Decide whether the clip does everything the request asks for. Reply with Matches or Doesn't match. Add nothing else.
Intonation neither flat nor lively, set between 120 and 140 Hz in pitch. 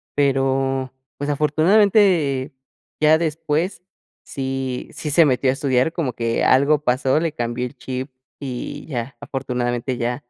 Matches